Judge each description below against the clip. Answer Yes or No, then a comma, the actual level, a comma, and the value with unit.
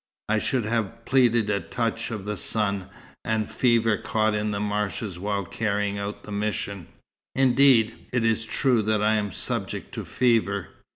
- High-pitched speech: No, low, 110 Hz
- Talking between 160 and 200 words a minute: Yes, average, 170 wpm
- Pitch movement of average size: No, narrow, 2.1 semitones